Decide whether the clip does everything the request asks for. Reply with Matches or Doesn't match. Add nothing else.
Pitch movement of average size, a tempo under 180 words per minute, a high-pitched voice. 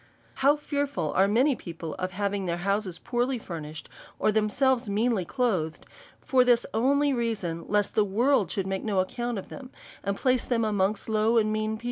Doesn't match